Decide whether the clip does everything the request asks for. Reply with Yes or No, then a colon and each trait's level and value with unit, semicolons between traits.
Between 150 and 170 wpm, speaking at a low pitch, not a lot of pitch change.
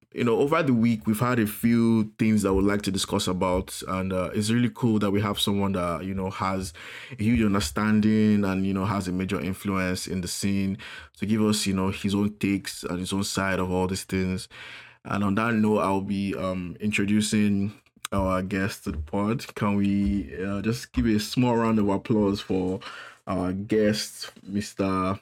No: fast, 205 wpm; low, 100 Hz; narrow, 2.1 semitones